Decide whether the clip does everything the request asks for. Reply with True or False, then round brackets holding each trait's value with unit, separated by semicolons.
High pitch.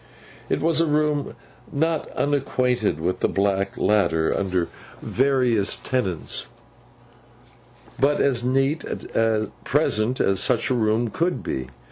False (120 Hz)